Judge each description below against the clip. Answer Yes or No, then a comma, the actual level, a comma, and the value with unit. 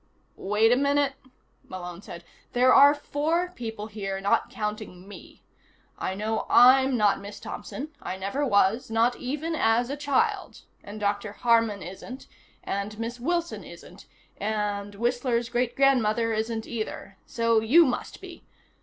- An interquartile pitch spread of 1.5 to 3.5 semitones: No, average, 4.3 semitones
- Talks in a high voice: Yes, high, 230 Hz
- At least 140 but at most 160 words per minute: Yes, average, 145 wpm